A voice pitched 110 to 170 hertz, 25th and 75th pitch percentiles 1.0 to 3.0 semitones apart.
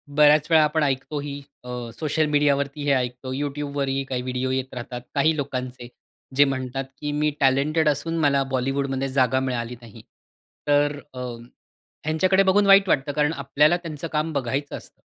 Yes: medium, 140 Hz; narrow, 2.5 semitones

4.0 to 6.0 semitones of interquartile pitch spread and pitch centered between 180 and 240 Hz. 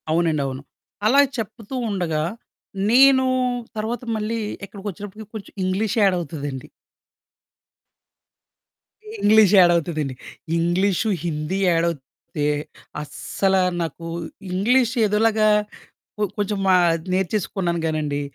Yes: average, 4.7 semitones; high, 190 Hz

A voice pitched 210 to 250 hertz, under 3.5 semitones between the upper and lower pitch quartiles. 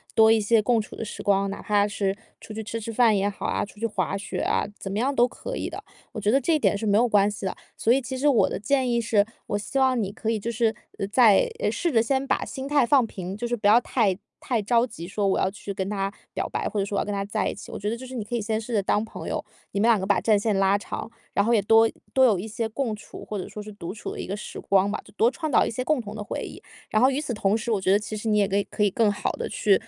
Yes: high, 215 Hz; average, 2.7 semitones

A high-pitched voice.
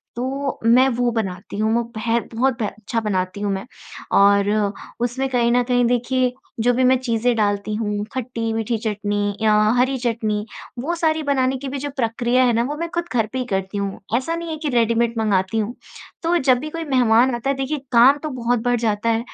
Yes: high, 240 Hz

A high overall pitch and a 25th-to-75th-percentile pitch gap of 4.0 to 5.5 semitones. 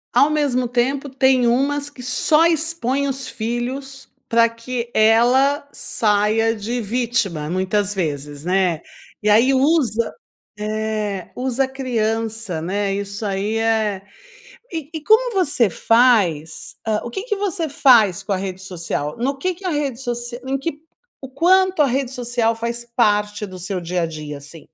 Yes: high, 235 Hz; average, 4.9 semitones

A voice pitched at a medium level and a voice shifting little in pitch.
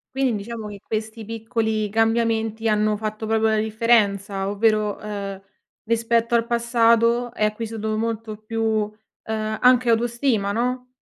No: high, 220 Hz; narrow, 1.5 semitones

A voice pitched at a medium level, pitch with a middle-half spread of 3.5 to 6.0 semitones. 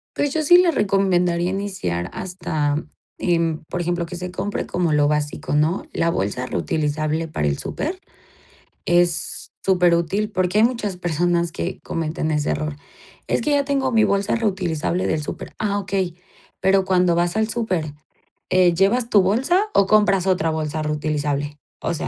Yes: medium, 175 Hz; average, 4.1 semitones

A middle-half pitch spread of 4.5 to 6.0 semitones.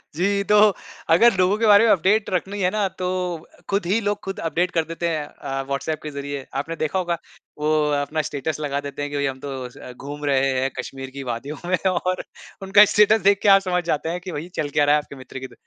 Yes: average, 5.2 semitones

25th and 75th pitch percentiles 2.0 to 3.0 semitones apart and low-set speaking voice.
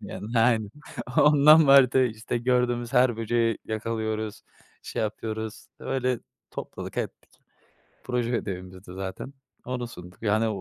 Yes: narrow, 2.5 semitones; low, 115 Hz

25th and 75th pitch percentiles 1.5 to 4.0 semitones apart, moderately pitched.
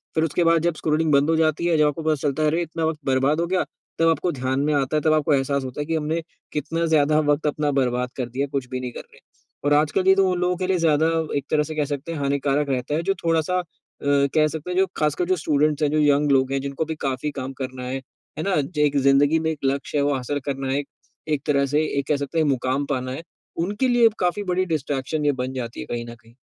Yes: average, 2.9 semitones; medium, 150 Hz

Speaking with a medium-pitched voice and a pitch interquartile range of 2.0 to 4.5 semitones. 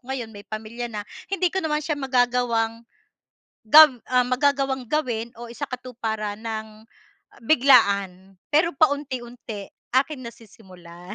No: high, 240 Hz; average, 4.1 semitones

